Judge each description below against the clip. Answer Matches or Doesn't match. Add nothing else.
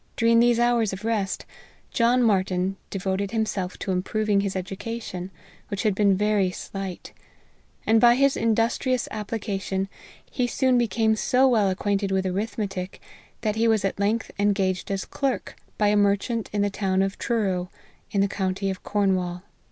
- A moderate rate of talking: Matches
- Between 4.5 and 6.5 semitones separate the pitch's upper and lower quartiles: Doesn't match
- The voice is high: Matches